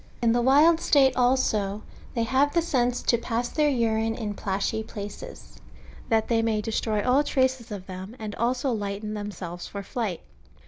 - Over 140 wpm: Yes, average, 170 wpm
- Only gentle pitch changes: No, average, 3.7 semitones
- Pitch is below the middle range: No, high, 225 Hz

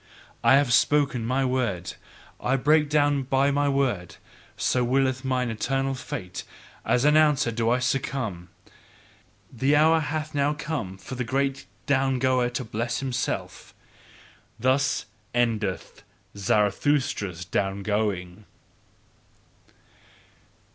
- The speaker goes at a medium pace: No, slow, 110 wpm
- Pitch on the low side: Yes, low, 130 Hz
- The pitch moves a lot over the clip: No, average, 3.9 semitones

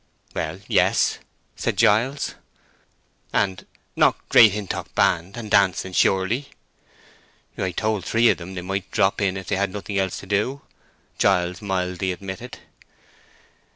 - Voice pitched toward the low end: Yes, very low, 95 Hz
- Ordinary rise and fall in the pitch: No, narrow, 2.1 semitones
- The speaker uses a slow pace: Yes, slow, 125 wpm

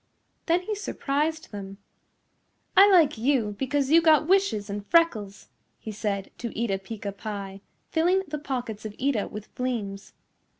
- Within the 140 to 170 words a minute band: Yes, average, 145 wpm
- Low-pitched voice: No, high, 245 Hz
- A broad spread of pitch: Yes, wide, 7.4 semitones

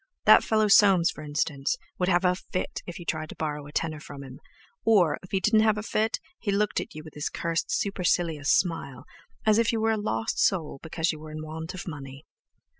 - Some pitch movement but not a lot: Yes, average, 4.7 semitones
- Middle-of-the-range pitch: Yes, medium, 170 Hz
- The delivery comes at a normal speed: No, fast, 225 wpm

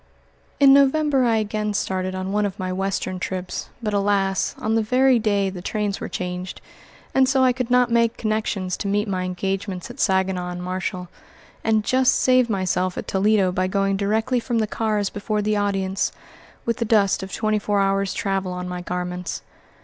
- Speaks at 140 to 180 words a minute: No, average, 190 wpm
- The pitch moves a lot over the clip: No, average, 3.0 semitones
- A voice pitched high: Yes, high, 200 Hz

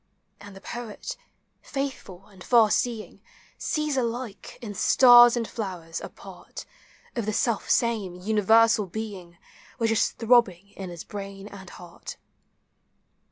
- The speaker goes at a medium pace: No, slow, 130 wpm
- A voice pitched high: Yes, high, 215 Hz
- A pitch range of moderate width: Yes, average, 3.5 semitones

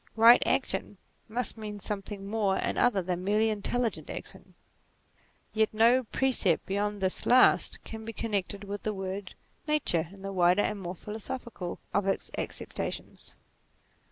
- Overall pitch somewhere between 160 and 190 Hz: No, high, 205 Hz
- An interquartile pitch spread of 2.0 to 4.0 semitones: Yes, narrow, 2.5 semitones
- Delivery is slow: No, average, 145 wpm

